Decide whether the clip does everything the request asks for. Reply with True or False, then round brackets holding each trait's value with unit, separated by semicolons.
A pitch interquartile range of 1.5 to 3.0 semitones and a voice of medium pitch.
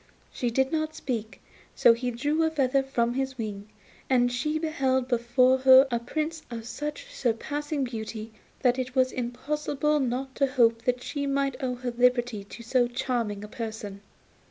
False (2.7 semitones; 255 Hz)